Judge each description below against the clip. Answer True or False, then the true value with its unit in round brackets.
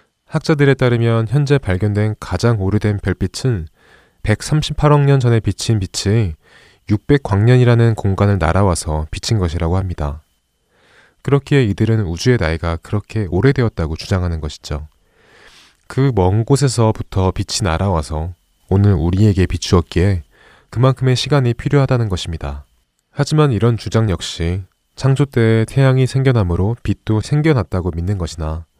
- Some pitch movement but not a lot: False (5.8 semitones)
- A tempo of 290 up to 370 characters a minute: True (315 characters per minute)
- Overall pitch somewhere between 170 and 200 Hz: False (105 Hz)